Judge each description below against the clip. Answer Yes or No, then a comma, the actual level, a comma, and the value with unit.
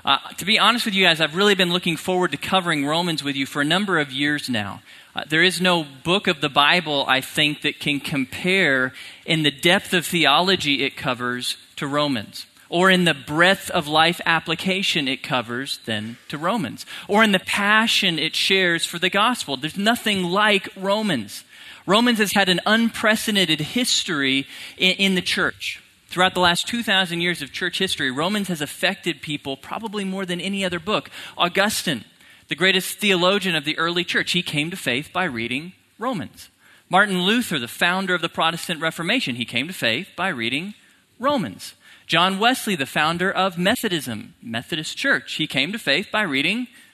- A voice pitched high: No, medium, 175 Hz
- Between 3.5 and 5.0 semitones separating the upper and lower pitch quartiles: Yes, average, 4.5 semitones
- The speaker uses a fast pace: No, average, 180 wpm